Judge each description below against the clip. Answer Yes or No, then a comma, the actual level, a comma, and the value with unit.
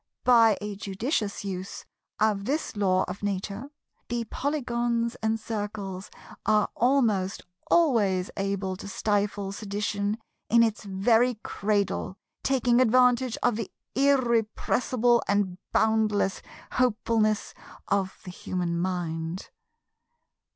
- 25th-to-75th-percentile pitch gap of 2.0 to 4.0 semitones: Yes, average, 3.3 semitones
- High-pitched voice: Yes, high, 210 Hz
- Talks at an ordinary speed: No, slow, 105 wpm